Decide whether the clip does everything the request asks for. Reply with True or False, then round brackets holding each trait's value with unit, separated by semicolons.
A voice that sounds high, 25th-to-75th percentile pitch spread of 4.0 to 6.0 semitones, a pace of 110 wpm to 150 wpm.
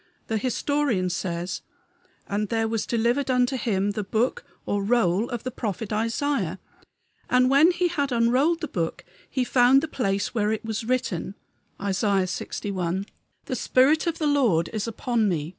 False (225 Hz; 4.4 semitones; 160 wpm)